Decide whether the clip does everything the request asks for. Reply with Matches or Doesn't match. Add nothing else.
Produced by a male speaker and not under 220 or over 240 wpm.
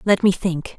Doesn't match